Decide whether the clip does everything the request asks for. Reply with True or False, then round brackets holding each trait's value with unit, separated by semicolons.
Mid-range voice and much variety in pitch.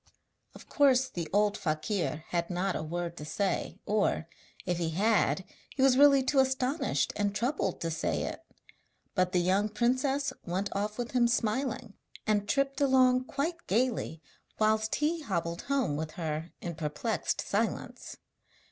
False (210 Hz; 6.8 semitones)